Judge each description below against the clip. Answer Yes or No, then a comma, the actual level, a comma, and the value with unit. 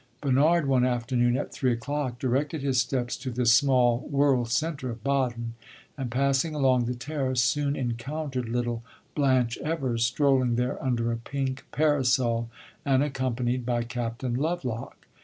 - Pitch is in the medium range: No, low, 130 Hz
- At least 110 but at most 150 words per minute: Yes, average, 145 wpm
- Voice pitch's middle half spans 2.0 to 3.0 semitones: Yes, narrow, 2.5 semitones